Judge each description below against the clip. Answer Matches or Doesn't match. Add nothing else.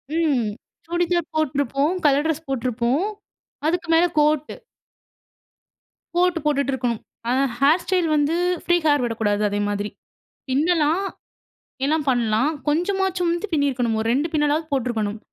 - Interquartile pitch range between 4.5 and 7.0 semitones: Matches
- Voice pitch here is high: Matches